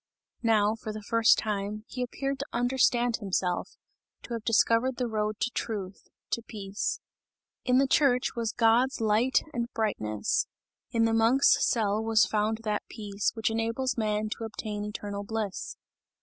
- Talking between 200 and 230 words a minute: No, average, 155 wpm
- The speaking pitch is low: No, high, 225 Hz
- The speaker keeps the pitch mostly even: Yes, narrow, 2.3 semitones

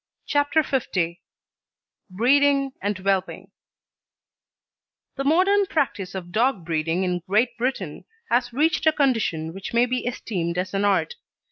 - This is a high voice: Yes, high, 225 Hz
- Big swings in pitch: Yes, wide, 6.8 semitones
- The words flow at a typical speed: No, slow, 130 wpm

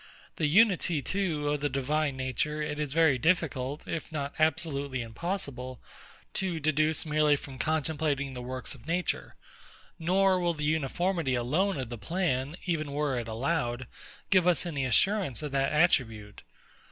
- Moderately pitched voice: Yes, medium, 150 Hz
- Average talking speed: Yes, average, 155 wpm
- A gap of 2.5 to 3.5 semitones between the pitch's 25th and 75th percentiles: No, average, 3.9 semitones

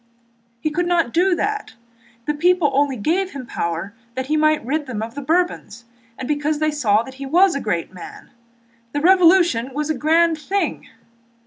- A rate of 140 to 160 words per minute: No, average, 185 wpm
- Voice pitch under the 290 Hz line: No, very high, 300 Hz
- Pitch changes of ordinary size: Yes, average, 4.8 semitones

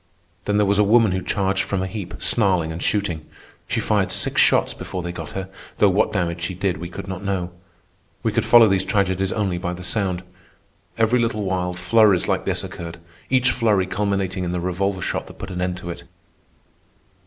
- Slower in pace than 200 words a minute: No, fast, 205 wpm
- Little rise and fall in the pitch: Yes, narrow, 2.3 semitones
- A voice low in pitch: Yes, very low, 95 Hz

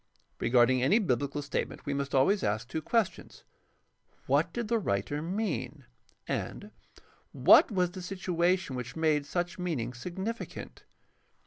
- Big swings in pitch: Yes, wide, 6.2 semitones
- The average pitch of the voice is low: No, medium, 160 Hz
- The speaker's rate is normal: No, slow, 130 wpm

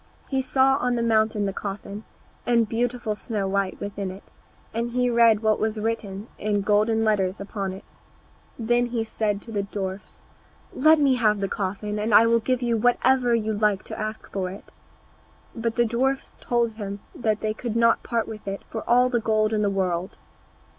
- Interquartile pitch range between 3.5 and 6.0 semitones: No, narrow, 2.6 semitones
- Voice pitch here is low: No, high, 220 Hz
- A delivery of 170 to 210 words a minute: Yes, average, 190 wpm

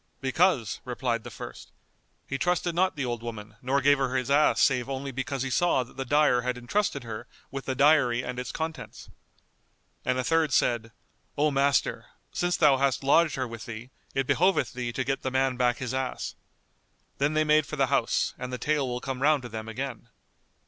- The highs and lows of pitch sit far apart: No, average, 2.8 semitones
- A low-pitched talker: Yes, low, 130 Hz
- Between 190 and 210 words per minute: Yes, fast, 205 wpm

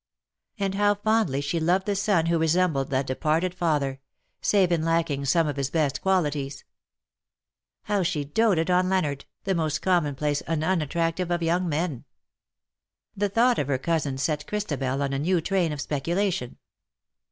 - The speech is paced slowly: No, average, 165 wpm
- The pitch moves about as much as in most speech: Yes, average, 4.4 semitones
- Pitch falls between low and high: Yes, medium, 165 Hz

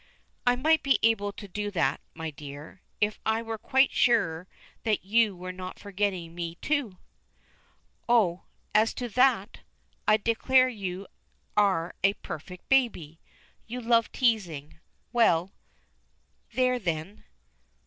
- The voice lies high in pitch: Yes, high, 205 Hz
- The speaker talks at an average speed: No, slow, 130 wpm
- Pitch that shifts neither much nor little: Yes, average, 4.7 semitones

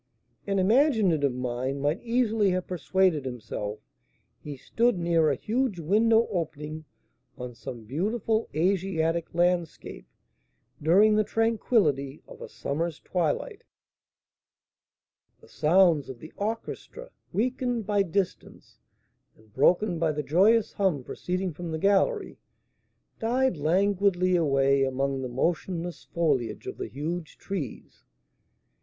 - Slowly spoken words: Yes, slow, 115 wpm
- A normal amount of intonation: No, wide, 5.9 semitones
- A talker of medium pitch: Yes, medium, 175 Hz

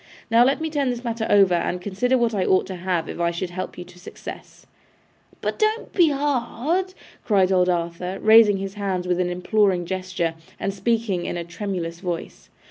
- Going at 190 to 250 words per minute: Yes, average, 195 wpm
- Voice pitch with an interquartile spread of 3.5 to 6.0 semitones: Yes, average, 4.5 semitones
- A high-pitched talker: Yes, high, 195 Hz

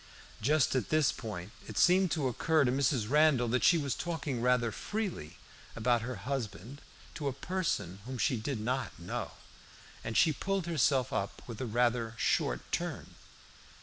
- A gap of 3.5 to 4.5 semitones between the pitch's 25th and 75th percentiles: No, average, 5.0 semitones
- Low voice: Yes, low, 130 Hz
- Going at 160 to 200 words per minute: Yes, average, 165 wpm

